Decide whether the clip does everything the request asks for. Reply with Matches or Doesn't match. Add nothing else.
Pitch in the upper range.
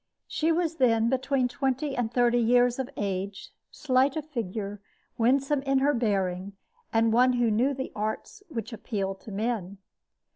Matches